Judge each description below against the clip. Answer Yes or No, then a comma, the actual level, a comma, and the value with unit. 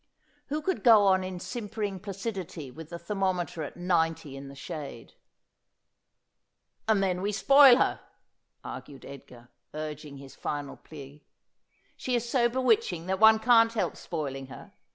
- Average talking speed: Yes, average, 155 wpm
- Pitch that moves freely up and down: Yes, wide, 6.7 semitones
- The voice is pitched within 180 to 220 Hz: Yes, medium, 185 Hz